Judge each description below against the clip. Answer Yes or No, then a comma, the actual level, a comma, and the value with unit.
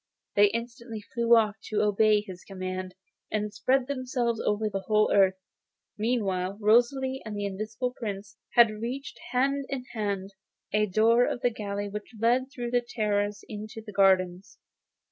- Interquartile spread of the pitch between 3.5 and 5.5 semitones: No, average, 2.8 semitones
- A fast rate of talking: No, average, 155 wpm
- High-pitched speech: Yes, high, 215 Hz